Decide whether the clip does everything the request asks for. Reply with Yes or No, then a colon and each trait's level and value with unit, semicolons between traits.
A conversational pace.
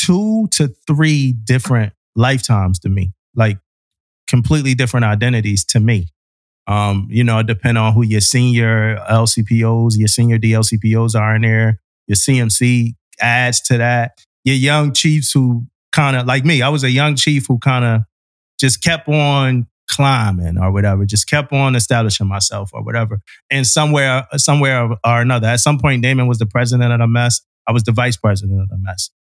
Yes: average, 175 wpm